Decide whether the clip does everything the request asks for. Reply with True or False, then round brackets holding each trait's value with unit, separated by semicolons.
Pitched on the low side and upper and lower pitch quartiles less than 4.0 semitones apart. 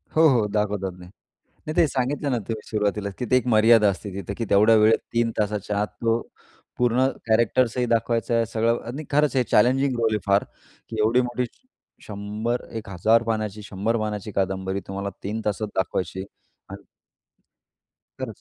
True (110 Hz; 2.6 semitones)